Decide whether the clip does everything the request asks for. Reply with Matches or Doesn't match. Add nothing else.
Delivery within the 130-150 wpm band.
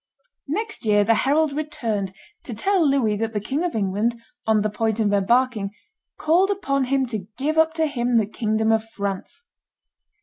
Doesn't match